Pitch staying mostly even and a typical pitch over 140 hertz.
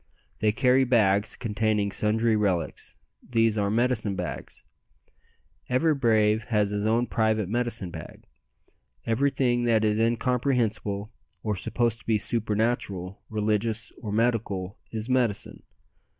No: narrow, 2.2 semitones; low, 110 Hz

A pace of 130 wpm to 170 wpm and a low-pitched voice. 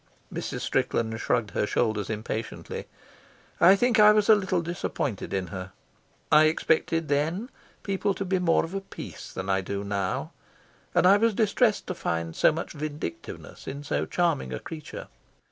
No: average, 165 wpm; medium, 155 Hz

